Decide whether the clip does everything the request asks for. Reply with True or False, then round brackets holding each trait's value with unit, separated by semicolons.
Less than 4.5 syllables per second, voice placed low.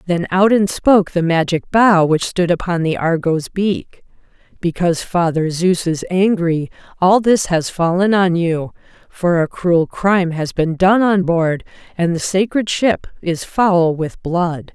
False (4.0 syllables/s; 175 Hz)